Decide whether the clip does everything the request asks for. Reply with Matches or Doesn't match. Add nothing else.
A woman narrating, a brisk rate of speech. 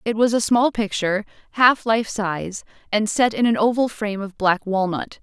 Doesn't match